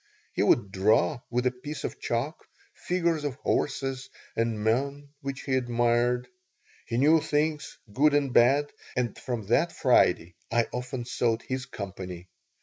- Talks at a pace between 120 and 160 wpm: Yes, average, 145 wpm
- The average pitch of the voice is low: Yes, low, 125 Hz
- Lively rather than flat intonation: No, average, 3.4 semitones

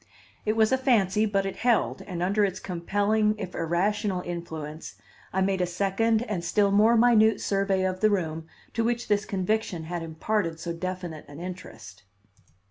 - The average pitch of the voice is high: Yes, high, 195 Hz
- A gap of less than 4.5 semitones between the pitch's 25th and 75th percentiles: Yes, average, 3.6 semitones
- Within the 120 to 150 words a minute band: No, average, 170 wpm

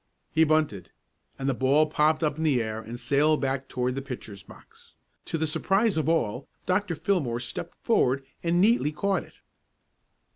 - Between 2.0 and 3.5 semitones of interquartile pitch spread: No, average, 4.1 semitones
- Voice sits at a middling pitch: Yes, medium, 150 Hz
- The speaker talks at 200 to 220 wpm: No, average, 175 wpm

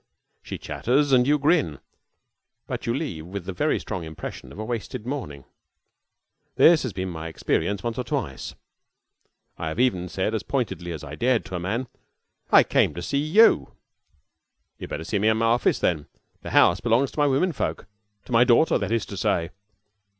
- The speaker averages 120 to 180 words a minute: No, average, 190 wpm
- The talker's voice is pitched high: No, low, 110 Hz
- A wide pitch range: Yes, wide, 6.7 semitones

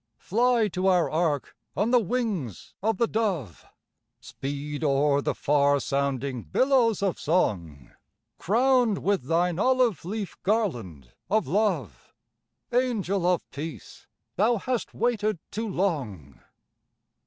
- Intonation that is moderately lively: No, wide, 7.7 semitones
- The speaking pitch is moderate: Yes, medium, 180 Hz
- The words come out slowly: Yes, slow, 120 wpm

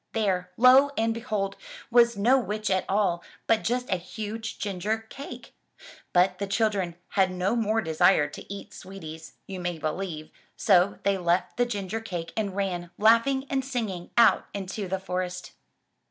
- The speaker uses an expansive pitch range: No, average, 3.6 semitones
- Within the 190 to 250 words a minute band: No, average, 165 wpm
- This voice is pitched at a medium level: No, high, 200 Hz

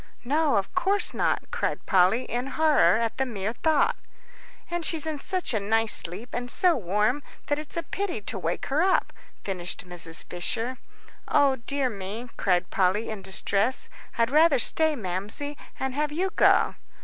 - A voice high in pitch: Yes, high, 245 Hz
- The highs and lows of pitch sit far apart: Yes, wide, 7.2 semitones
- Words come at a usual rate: Yes, average, 170 wpm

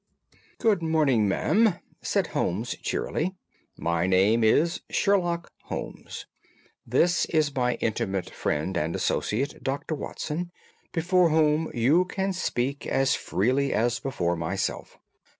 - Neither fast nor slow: No, slow, 115 wpm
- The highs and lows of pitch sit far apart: Yes, wide, 7.6 semitones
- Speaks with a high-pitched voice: No, low, 135 Hz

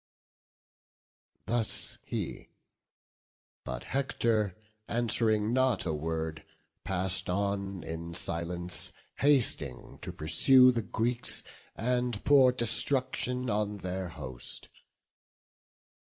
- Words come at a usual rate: No, slow, 85 wpm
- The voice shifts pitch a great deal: Yes, wide, 5.8 semitones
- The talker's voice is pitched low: Yes, low, 105 Hz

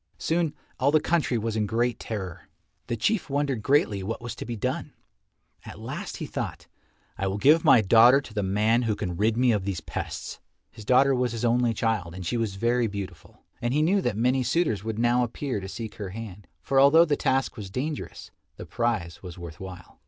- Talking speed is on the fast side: Yes, fast, 210 wpm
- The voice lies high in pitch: No, low, 115 Hz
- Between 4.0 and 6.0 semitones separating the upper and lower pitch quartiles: Yes, average, 4.3 semitones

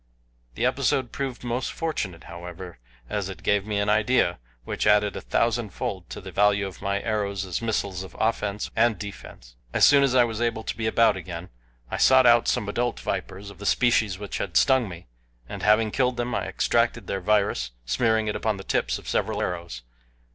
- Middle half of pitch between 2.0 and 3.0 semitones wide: No, average, 3.5 semitones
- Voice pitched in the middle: No, low, 105 Hz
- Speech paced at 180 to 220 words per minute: Yes, average, 200 wpm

